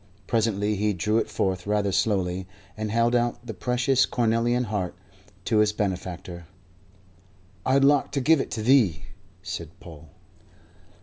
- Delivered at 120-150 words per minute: Yes, average, 140 wpm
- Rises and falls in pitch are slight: No, average, 4.3 semitones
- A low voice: Yes, low, 105 Hz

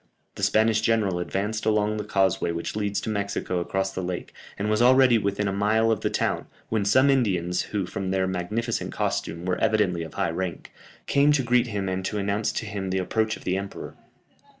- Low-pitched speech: Yes, low, 100 Hz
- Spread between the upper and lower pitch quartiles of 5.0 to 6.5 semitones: No, average, 2.8 semitones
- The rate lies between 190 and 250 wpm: Yes, fast, 205 wpm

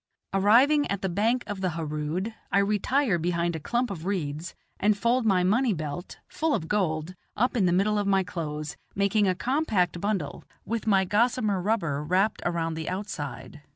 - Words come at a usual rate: Yes, average, 180 wpm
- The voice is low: No, high, 190 Hz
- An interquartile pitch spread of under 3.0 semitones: No, average, 4.2 semitones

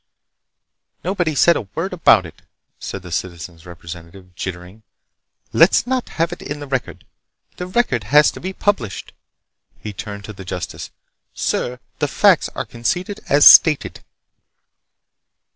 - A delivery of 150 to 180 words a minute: No, average, 140 wpm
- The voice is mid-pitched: No, low, 120 Hz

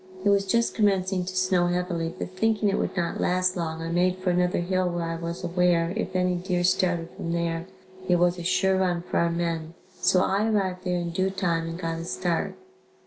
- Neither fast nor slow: No, fast, 220 wpm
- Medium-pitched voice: Yes, medium, 180 Hz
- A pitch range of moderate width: No, narrow, 1.6 semitones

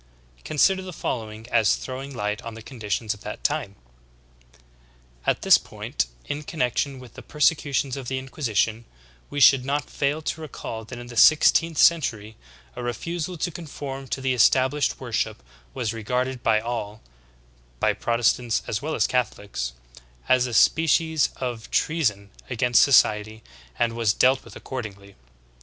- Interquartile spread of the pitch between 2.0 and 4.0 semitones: No, average, 4.4 semitones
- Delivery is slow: No, average, 150 wpm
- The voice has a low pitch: Yes, low, 125 Hz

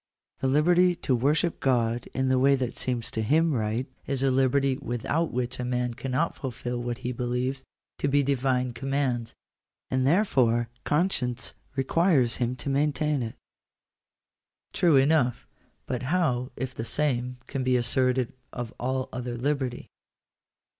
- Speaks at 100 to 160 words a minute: Yes, average, 145 wpm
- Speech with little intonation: Yes, narrow, 2.3 semitones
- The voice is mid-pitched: No, low, 130 Hz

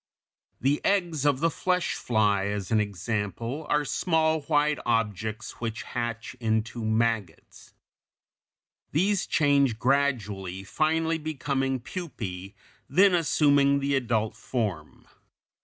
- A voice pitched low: Yes, low, 130 Hz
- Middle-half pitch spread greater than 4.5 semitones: Yes, wide, 5.5 semitones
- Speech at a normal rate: No, slow, 115 wpm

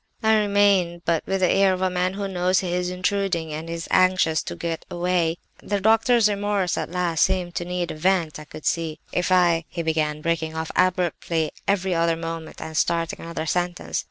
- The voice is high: No, medium, 175 Hz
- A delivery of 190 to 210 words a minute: Yes, average, 200 wpm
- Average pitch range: No, narrow, 2.3 semitones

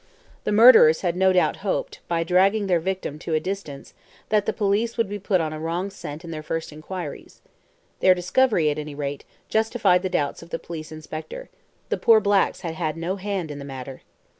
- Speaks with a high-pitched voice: No, medium, 180 Hz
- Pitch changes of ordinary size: Yes, average, 4.2 semitones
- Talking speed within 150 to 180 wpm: No, fast, 205 wpm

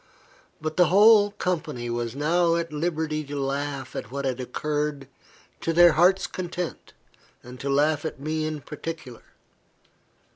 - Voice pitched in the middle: Yes, medium, 155 Hz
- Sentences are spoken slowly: No, average, 145 wpm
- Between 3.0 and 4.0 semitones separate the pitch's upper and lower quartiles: Yes, average, 3.3 semitones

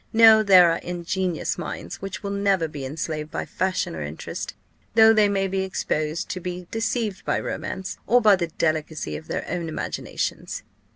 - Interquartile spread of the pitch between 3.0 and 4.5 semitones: Yes, average, 3.9 semitones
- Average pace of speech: Yes, average, 175 wpm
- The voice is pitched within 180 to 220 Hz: Yes, medium, 185 Hz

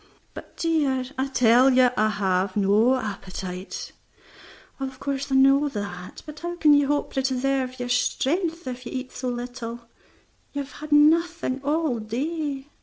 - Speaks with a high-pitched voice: Yes, very high, 265 Hz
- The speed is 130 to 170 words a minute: Yes, average, 165 wpm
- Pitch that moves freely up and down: No, average, 3.4 semitones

